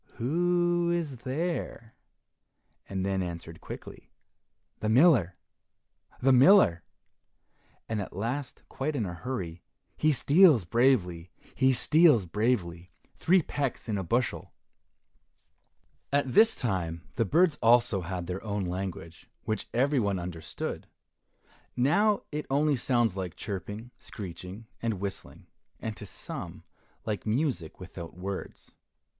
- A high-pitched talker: No, low, 115 Hz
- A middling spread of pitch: No, wide, 7.1 semitones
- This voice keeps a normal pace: No, slow, 120 wpm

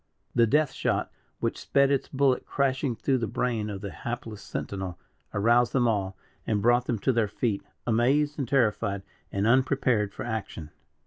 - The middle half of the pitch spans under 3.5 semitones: No, average, 4.0 semitones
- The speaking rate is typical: Yes, average, 170 wpm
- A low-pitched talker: Yes, low, 120 Hz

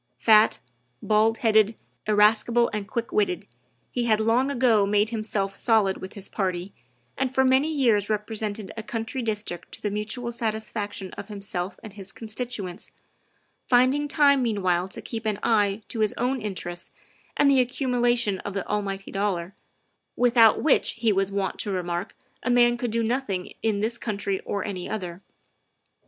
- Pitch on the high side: Yes, high, 215 Hz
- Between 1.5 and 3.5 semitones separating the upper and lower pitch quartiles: Yes, average, 3.2 semitones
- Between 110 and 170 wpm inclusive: Yes, average, 160 wpm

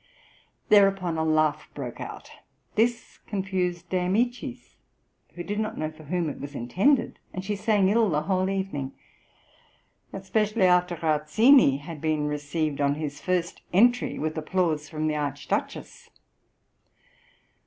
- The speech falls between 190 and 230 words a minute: No, slow, 135 wpm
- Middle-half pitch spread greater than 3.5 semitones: Yes, average, 4.4 semitones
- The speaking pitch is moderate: Yes, medium, 175 Hz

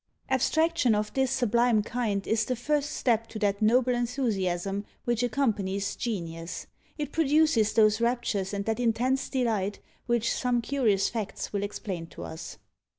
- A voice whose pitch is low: No, high, 230 Hz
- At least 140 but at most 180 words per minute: Yes, average, 150 wpm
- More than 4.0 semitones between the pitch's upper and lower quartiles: No, average, 3.6 semitones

